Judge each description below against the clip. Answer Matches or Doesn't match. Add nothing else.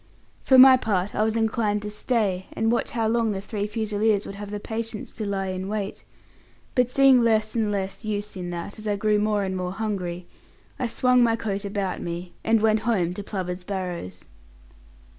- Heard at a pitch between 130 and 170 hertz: Doesn't match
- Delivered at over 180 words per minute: Matches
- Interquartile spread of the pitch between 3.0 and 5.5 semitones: Doesn't match